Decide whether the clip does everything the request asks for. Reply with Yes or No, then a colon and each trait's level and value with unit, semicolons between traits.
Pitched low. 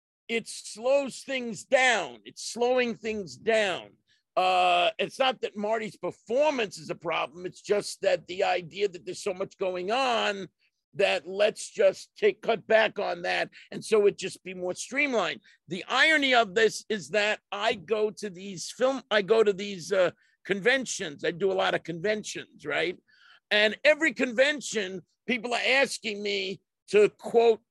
No: high, 210 Hz